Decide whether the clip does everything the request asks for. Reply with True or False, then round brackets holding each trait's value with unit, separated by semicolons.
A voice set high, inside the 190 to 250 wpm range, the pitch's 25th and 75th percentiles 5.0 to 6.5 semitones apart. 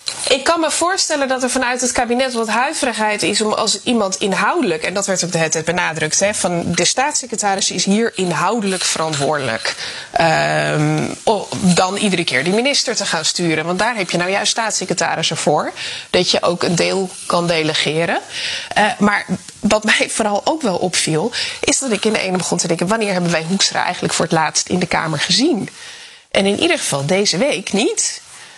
True (200 Hz; 195 wpm; 5.6 semitones)